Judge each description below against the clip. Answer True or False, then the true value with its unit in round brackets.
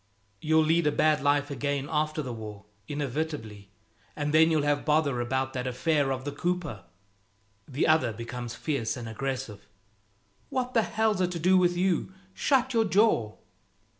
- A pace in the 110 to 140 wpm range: False (165 wpm)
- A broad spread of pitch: False (4.5 semitones)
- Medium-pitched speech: True (145 Hz)